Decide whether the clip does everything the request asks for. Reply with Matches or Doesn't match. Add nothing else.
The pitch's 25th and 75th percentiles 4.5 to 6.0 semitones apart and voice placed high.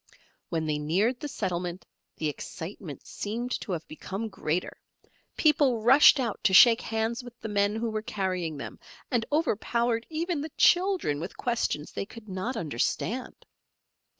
Matches